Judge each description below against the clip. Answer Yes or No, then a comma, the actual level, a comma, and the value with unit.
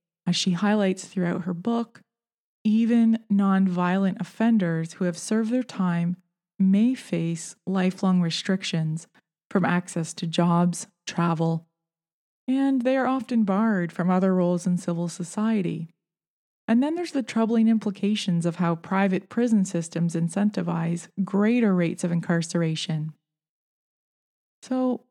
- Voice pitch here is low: No, medium, 185 Hz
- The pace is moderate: No, slow, 120 wpm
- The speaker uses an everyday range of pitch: Yes, average, 4.2 semitones